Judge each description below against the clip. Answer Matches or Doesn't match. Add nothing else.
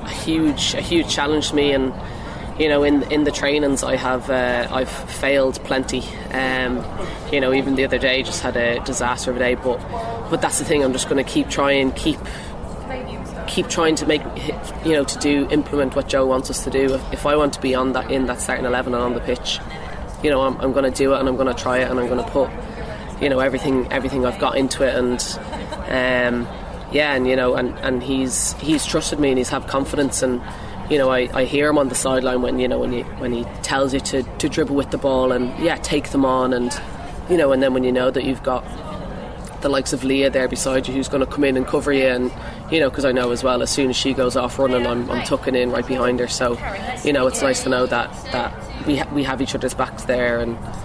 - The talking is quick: Matches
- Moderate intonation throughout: Doesn't match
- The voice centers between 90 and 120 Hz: Doesn't match